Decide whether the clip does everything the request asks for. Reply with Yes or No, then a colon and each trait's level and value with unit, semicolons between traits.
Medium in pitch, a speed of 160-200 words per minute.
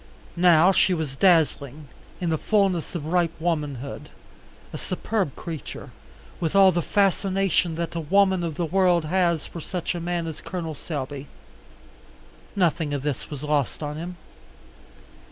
No: medium, 170 Hz; average, 150 wpm